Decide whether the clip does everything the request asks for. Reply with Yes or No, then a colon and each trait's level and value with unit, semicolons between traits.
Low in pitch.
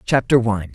Yes: low, 110 Hz